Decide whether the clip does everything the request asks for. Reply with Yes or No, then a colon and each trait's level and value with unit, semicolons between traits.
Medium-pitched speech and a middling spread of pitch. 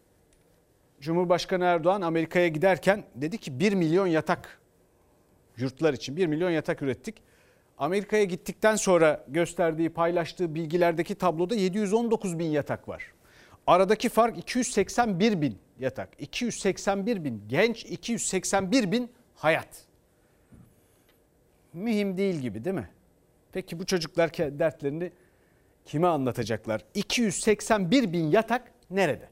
Yes: medium, 180 Hz; average, 4.3 semitones